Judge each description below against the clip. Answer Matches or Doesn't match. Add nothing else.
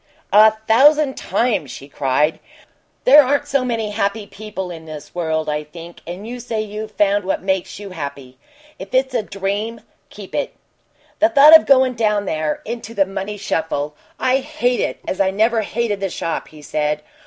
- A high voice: Matches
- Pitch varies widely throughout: Matches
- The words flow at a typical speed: Matches